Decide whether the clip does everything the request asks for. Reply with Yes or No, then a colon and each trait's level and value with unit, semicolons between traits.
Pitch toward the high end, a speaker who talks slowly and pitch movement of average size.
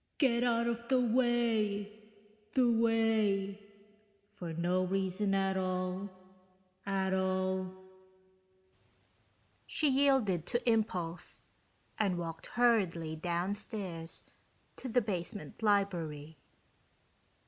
Yes: high, 195 Hz; slow, 90 wpm; average, 4.0 semitones